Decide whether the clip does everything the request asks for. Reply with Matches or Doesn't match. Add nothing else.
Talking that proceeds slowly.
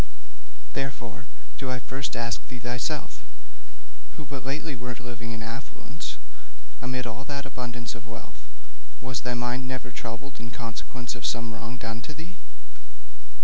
Doesn't match